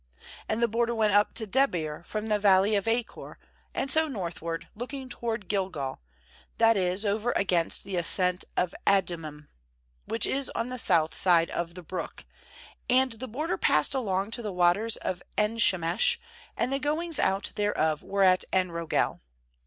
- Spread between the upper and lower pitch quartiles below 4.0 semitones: No, average, 4.6 semitones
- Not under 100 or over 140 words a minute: No, average, 170 wpm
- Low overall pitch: No, high, 205 Hz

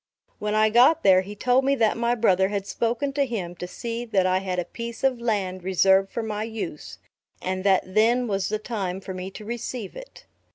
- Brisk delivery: Yes, fast, 215 wpm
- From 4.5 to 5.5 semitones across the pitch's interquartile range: No, average, 3.8 semitones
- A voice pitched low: No, high, 210 Hz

